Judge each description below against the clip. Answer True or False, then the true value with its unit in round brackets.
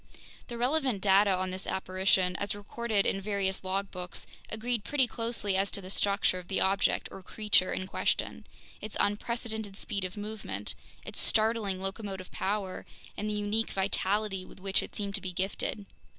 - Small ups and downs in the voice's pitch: True (2.2 semitones)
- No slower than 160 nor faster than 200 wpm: True (165 wpm)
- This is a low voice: False (200 Hz)